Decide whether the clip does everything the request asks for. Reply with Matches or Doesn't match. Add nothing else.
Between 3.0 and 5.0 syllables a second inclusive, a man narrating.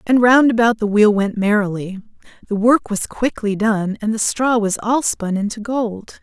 Doesn't match